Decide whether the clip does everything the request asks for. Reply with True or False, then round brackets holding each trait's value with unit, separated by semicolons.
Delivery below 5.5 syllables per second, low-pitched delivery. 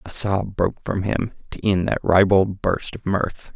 True (4.3 syllables/s; 95 Hz)